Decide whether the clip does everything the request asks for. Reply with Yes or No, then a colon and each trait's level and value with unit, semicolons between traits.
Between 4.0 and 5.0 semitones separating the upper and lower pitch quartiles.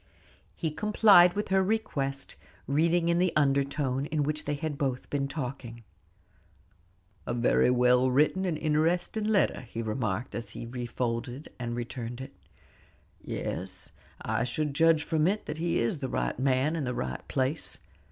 Yes: average, 4.7 semitones